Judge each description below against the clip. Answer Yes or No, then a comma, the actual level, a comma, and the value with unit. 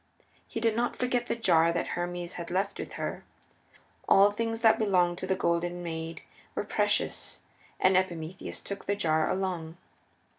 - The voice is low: No, medium, 185 Hz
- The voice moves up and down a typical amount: Yes, average, 3.2 semitones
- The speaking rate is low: No, average, 160 wpm